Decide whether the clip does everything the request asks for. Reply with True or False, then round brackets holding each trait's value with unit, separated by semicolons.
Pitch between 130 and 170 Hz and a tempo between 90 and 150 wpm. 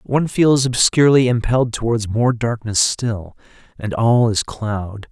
False (115 Hz; 140 wpm)